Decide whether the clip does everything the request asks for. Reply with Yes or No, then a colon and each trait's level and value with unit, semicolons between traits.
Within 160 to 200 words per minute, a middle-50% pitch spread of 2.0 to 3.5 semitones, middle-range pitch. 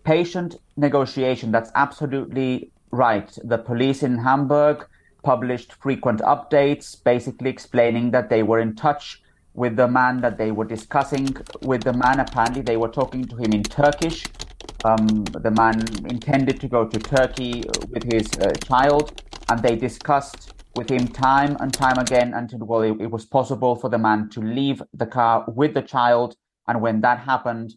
No: average, 170 wpm; average, 2.8 semitones; low, 125 Hz